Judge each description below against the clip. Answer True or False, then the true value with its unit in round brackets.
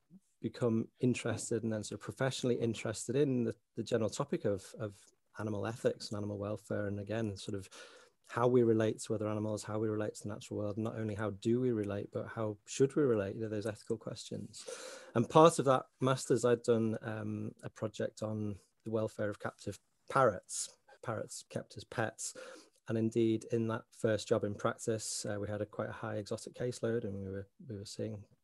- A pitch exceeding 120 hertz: False (110 Hz)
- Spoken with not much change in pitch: True (2.0 semitones)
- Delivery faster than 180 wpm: True (205 wpm)